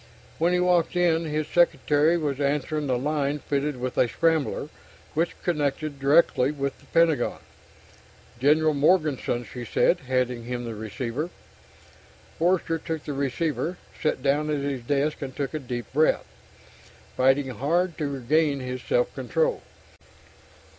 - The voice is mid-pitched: Yes, medium, 145 Hz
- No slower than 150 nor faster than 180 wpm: No, average, 140 wpm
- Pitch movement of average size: Yes, average, 3.5 semitones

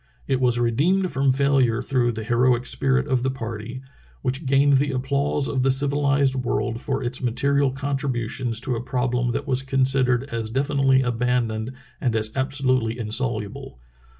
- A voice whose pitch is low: Yes, low, 130 Hz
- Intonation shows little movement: Yes, narrow, 2.2 semitones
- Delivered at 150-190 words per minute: Yes, average, 160 wpm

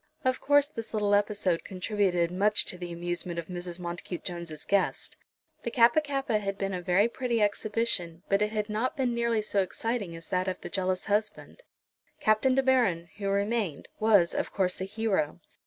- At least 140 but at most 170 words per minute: No, average, 185 wpm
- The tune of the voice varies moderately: Yes, average, 4.1 semitones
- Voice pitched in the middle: No, high, 200 Hz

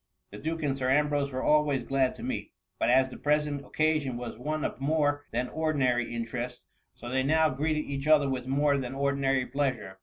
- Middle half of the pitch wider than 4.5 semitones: No, average, 2.7 semitones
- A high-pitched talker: No, medium, 140 Hz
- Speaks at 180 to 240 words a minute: Yes, average, 195 wpm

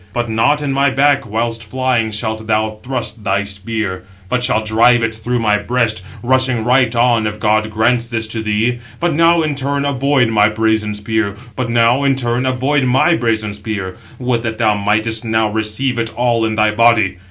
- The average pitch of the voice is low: Yes, low, 115 Hz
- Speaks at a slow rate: No, average, 165 wpm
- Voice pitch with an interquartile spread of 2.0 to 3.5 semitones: Yes, narrow, 2.6 semitones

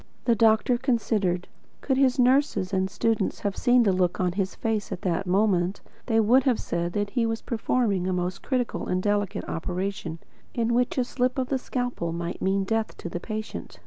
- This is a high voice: Yes, high, 205 Hz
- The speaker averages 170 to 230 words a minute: Yes, average, 195 wpm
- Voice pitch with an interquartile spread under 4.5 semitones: No, average, 4.8 semitones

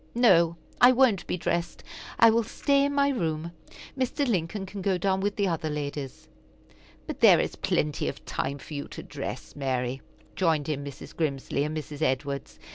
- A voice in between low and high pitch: Yes, medium, 170 Hz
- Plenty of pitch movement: Yes, wide, 6.3 semitones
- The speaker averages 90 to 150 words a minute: No, average, 180 wpm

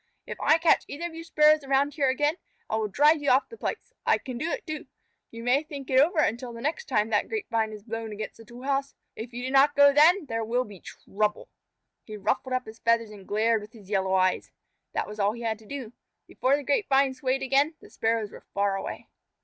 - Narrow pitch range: No, average, 4.7 semitones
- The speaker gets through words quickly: Yes, fast, 240 wpm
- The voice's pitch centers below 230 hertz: No, very high, 255 Hz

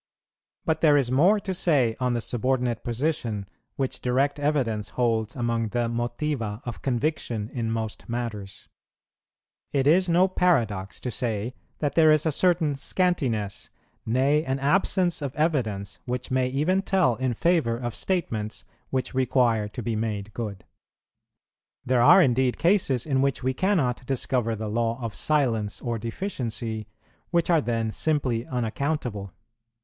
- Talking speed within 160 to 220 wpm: No, average, 145 wpm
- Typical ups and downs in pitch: Yes, average, 4.7 semitones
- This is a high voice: No, low, 125 Hz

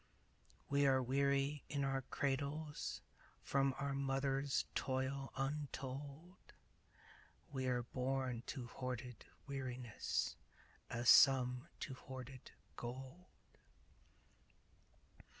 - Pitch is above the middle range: No, low, 135 Hz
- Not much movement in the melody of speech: Yes, narrow, 1.5 semitones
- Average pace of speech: No, slow, 85 wpm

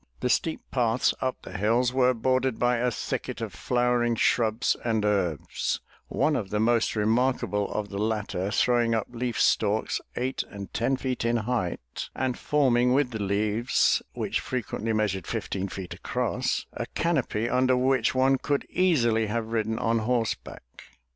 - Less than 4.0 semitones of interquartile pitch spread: Yes, average, 2.9 semitones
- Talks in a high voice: No, low, 115 Hz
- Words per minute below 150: No, average, 160 wpm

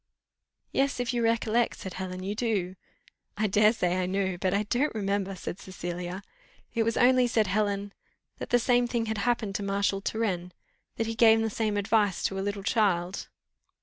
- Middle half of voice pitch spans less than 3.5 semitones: Yes, average, 3.0 semitones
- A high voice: Yes, high, 205 Hz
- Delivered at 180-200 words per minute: Yes, average, 185 wpm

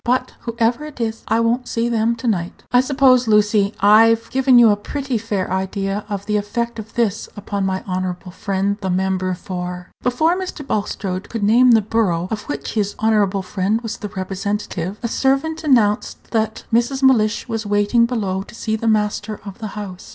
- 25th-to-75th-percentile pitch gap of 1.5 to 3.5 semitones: Yes, average, 3.0 semitones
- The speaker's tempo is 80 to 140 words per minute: No, average, 190 wpm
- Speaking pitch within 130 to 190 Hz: No, high, 215 Hz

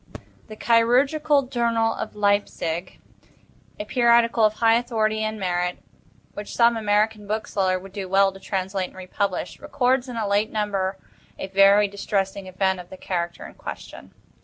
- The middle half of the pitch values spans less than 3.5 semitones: Yes, average, 3.1 semitones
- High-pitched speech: Yes, high, 205 Hz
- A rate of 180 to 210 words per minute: No, average, 155 wpm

